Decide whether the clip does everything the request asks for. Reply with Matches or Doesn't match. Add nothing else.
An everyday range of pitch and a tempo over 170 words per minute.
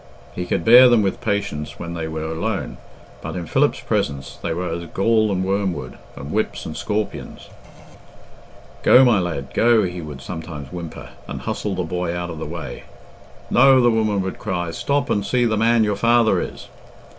Matches